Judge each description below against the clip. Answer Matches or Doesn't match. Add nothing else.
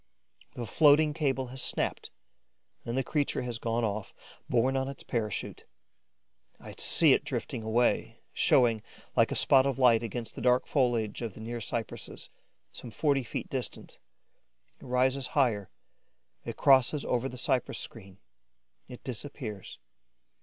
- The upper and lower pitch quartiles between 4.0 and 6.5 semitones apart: Doesn't match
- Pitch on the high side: Doesn't match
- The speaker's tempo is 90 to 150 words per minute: Matches